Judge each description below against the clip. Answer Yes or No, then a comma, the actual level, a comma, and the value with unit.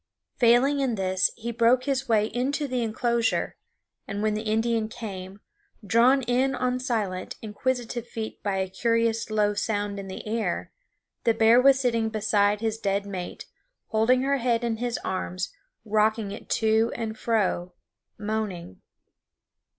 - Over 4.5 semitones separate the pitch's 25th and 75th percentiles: No, average, 2.7 semitones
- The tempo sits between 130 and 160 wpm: Yes, average, 150 wpm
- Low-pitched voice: No, high, 225 Hz